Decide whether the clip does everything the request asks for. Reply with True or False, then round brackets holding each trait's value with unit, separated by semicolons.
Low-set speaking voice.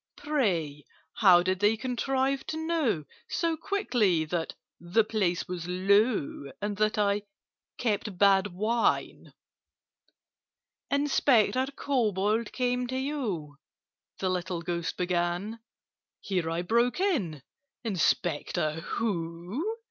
False (205 Hz)